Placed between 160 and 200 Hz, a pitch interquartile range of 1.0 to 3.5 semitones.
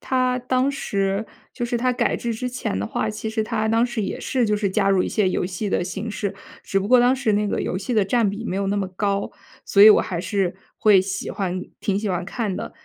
No: high, 210 Hz; average, 3.2 semitones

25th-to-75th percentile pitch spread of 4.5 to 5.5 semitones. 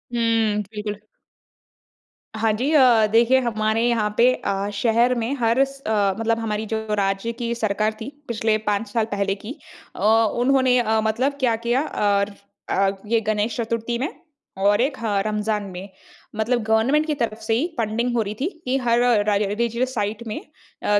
No: narrow, 2.4 semitones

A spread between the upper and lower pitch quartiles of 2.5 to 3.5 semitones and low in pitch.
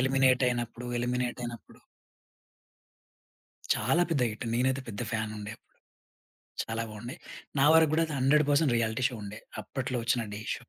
Yes: average, 2.9 semitones; low, 125 Hz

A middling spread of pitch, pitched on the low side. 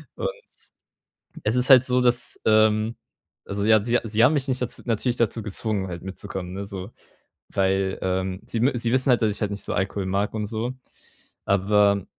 Yes: average, 3.4 semitones; low, 105 Hz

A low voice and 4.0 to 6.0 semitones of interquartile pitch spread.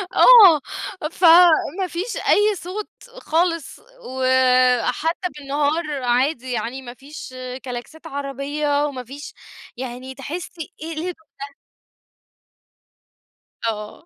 No: very high, 290 Hz; average, 4.5 semitones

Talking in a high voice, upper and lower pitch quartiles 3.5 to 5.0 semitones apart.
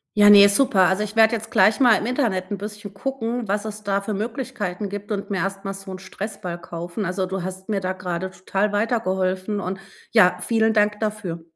No: high, 200 Hz; narrow, 2.4 semitones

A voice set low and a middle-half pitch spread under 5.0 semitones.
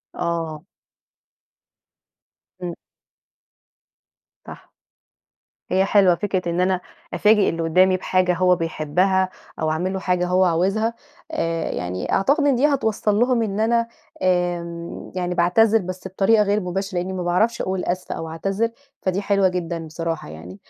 No: medium, 185 Hz; average, 2.9 semitones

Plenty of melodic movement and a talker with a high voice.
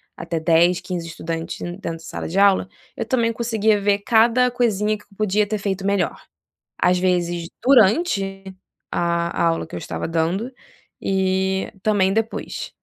No: average, 3.8 semitones; high, 195 Hz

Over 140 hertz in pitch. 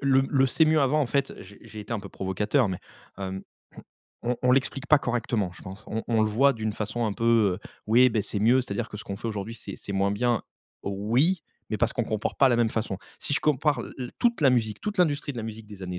No: low, 115 Hz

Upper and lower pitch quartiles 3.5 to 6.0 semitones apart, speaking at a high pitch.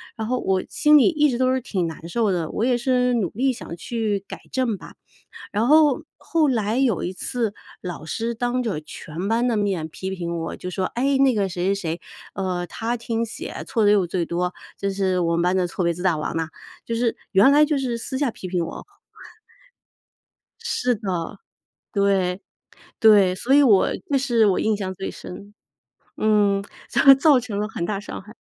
Yes: average, 4.9 semitones; high, 210 Hz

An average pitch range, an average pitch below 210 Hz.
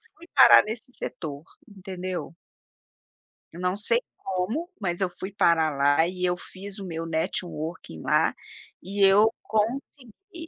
Yes: average, 4.2 semitones; medium, 185 Hz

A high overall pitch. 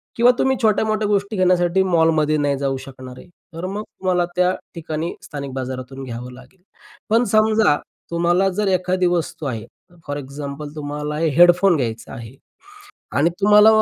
No: medium, 170 Hz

